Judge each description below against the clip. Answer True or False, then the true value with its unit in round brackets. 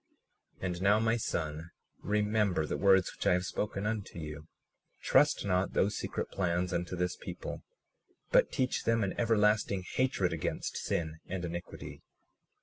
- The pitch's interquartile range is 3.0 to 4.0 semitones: True (3.4 semitones)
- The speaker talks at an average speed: True (150 wpm)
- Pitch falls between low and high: False (95 Hz)